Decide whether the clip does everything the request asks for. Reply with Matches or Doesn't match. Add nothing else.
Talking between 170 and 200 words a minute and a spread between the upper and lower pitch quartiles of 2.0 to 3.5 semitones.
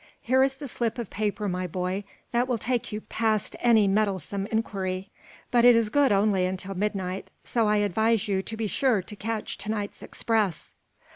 Matches